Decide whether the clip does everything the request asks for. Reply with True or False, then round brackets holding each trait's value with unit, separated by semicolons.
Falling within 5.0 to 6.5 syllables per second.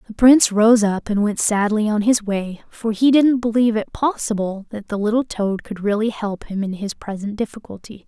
True (5.1 syllables/s)